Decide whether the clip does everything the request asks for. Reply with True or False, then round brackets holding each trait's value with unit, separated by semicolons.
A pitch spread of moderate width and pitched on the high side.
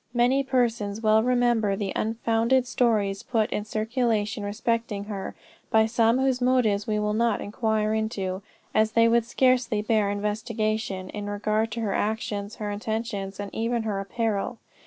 False (2.2 semitones; 220 Hz)